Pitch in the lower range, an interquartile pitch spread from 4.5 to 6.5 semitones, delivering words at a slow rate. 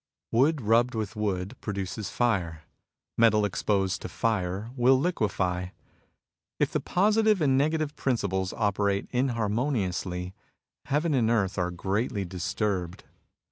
Yes: low, 105 Hz; average, 5.0 semitones; slow, 115 wpm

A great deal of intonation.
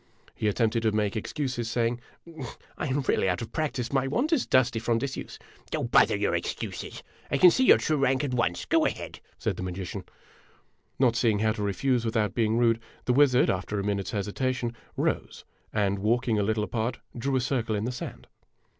No: average, 3.4 semitones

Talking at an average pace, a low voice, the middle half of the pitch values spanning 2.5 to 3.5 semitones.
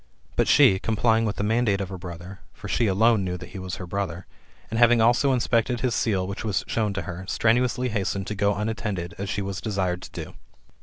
No: fast, 220 wpm; low, 100 Hz; average, 3.2 semitones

